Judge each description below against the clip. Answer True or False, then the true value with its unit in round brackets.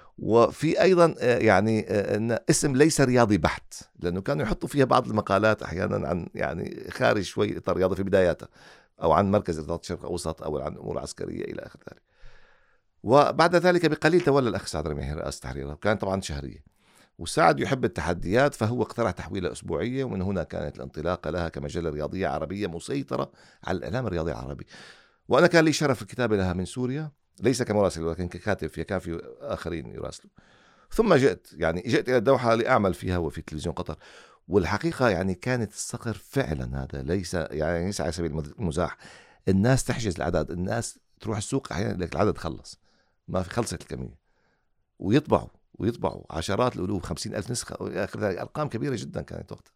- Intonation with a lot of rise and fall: True (6.4 semitones)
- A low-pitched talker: True (100 Hz)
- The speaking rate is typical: False (160 wpm)